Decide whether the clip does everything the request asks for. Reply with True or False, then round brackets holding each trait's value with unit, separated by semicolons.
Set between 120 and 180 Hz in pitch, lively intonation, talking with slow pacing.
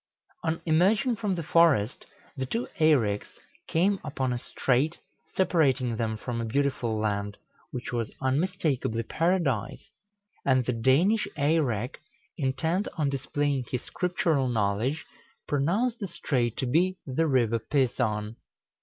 True (135 Hz; 5.8 semitones; 125 wpm)